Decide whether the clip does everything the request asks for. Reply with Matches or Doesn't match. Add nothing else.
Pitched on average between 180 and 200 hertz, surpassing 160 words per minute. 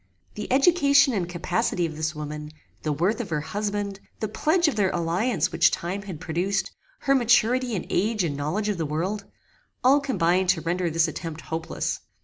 Matches